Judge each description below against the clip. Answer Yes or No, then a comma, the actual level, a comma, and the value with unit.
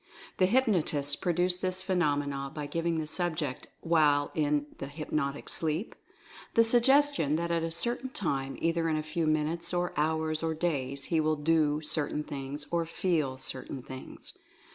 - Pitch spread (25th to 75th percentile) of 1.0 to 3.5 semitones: Yes, average, 2.9 semitones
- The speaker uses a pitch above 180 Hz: No, medium, 160 Hz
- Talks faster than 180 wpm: No, average, 165 wpm